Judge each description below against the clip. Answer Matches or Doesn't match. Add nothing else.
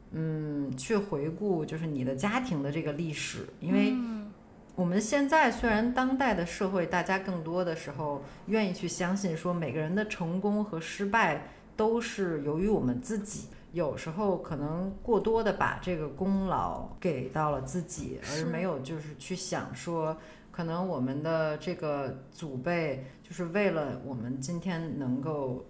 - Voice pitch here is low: Doesn't match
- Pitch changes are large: Doesn't match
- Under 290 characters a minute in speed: Matches